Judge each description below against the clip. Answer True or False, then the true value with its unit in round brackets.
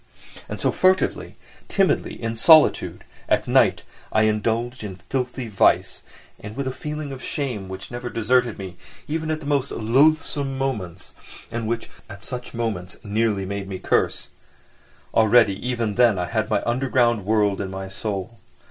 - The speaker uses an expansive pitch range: False (4.3 semitones)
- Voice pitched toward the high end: False (115 Hz)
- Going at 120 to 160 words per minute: True (155 wpm)